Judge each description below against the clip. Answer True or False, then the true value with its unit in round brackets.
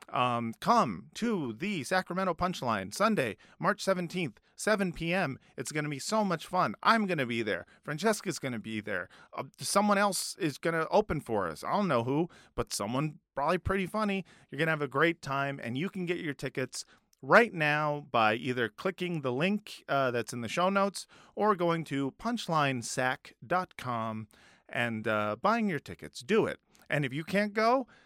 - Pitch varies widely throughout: True (6.9 semitones)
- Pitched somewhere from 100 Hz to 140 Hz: False (160 Hz)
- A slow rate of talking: False (190 wpm)